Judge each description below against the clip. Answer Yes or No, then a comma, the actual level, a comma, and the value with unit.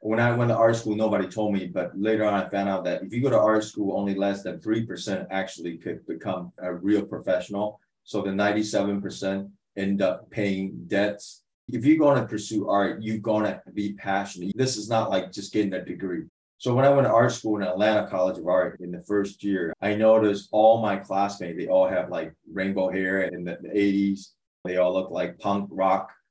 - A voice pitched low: Yes, low, 100 Hz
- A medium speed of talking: No, fast, 215 wpm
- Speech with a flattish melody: Yes, narrow, 2.1 semitones